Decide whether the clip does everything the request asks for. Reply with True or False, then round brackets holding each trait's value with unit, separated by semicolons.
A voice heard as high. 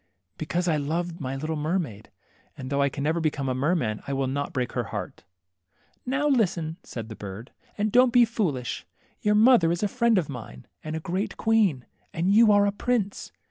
False (165 Hz)